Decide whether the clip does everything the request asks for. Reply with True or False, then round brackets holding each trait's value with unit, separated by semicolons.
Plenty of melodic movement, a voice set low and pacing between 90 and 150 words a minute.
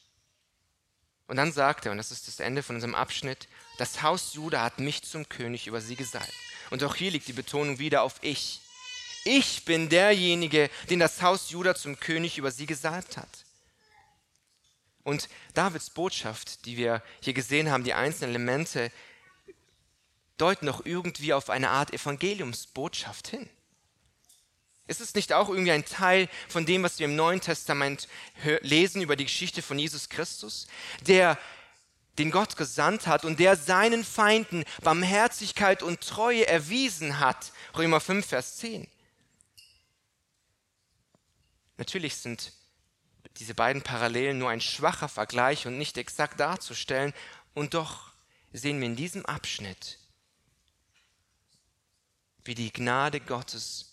False (6.5 semitones; 150 Hz; 140 wpm)